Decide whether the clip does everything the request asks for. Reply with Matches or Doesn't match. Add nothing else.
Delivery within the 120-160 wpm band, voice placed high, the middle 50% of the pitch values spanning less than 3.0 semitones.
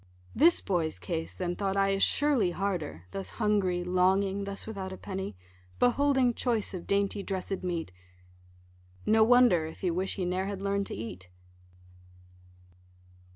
Matches